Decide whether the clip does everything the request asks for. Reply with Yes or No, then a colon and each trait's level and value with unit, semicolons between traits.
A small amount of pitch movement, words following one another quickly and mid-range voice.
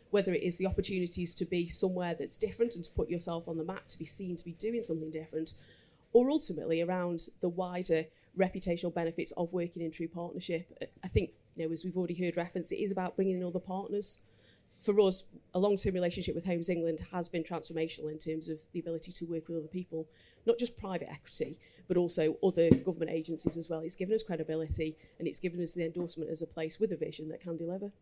Yes: narrow, 2.2 semitones; fast, 225 wpm; medium, 170 Hz